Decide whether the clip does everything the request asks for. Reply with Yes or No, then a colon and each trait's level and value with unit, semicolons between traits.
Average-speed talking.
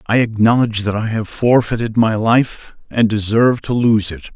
Yes: average, 180 wpm